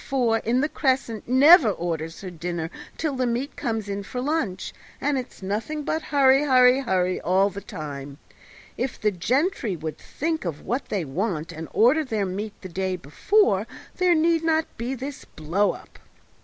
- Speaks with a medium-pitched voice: No, high, 225 Hz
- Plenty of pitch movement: Yes, wide, 7.1 semitones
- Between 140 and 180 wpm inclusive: Yes, average, 170 wpm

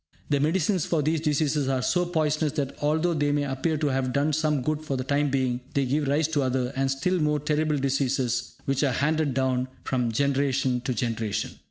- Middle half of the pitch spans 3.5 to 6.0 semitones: No, narrow, 2.6 semitones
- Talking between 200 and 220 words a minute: Yes, fast, 205 wpm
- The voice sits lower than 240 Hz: Yes, medium, 140 Hz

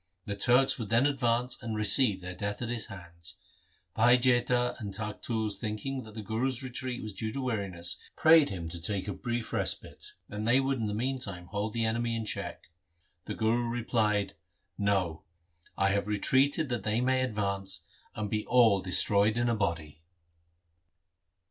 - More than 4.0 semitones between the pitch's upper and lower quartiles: No, average, 3.4 semitones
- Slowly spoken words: No, average, 175 wpm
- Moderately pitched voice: No, low, 110 Hz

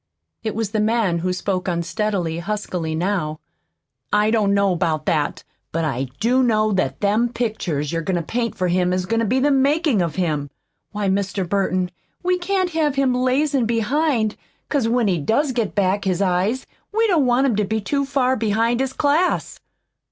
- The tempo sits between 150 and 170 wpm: No, average, 190 wpm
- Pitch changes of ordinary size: No, wide, 5.7 semitones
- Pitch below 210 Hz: No, high, 215 Hz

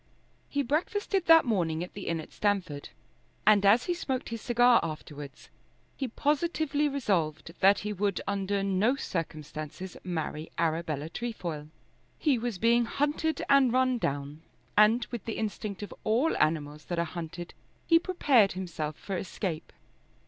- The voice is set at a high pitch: Yes, high, 200 Hz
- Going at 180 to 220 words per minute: No, average, 150 wpm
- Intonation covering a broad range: Yes, wide, 7.2 semitones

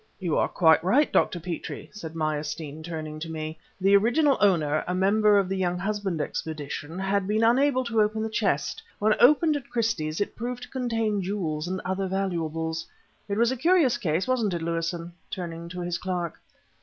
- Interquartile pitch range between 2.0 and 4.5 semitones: No, average, 5.1 semitones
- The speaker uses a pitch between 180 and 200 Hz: Yes, high, 190 Hz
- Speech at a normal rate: Yes, average, 180 wpm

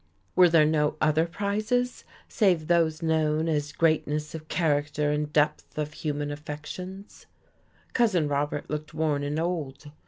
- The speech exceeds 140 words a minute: No, slow, 135 wpm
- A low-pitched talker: No, medium, 155 Hz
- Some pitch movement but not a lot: No, narrow, 2.3 semitones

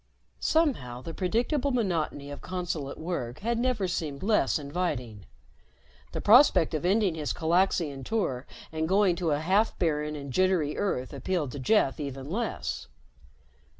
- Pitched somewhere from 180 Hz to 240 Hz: No, medium, 170 Hz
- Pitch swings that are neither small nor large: No, wide, 5.8 semitones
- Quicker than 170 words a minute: No, average, 150 wpm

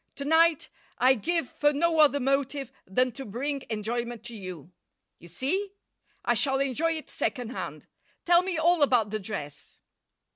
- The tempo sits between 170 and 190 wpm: No, average, 160 wpm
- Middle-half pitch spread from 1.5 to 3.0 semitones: No, wide, 5.5 semitones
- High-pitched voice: Yes, very high, 270 Hz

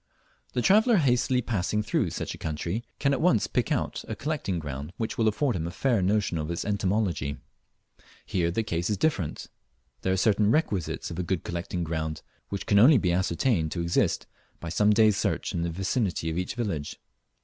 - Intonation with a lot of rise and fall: No, average, 5.0 semitones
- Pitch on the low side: Yes, very low, 95 Hz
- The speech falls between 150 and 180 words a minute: No, average, 195 wpm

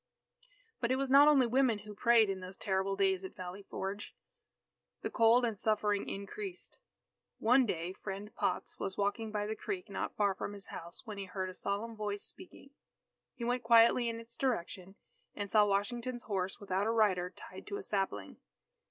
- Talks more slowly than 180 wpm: No, average, 185 wpm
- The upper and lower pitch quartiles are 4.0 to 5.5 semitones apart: No, average, 3.4 semitones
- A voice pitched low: No, high, 210 Hz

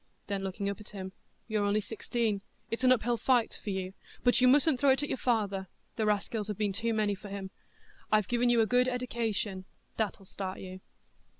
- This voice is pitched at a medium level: No, high, 215 Hz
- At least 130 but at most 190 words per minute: No, fast, 205 wpm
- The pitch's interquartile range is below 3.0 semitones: No, average, 3.4 semitones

